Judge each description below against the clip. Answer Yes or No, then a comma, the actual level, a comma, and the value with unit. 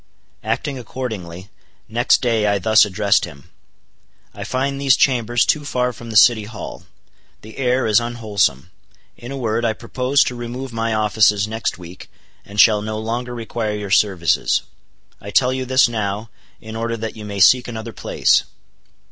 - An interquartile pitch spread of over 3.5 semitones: No, average, 2.9 semitones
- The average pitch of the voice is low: Yes, low, 115 Hz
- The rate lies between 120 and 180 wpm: Yes, average, 165 wpm